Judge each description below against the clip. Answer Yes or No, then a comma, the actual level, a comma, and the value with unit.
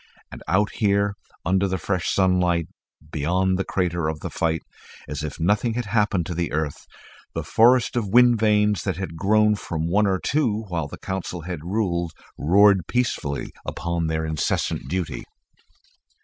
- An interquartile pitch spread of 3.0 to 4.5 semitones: Yes, average, 3.9 semitones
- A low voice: Yes, very low, 95 Hz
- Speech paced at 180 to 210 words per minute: No, average, 165 wpm